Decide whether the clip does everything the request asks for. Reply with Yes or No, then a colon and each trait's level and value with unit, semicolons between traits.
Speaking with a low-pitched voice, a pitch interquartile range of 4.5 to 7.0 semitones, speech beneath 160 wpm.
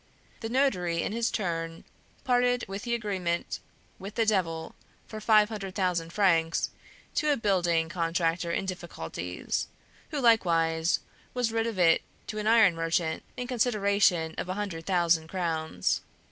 No: medium, 185 Hz; average, 4.8 semitones; average, 145 wpm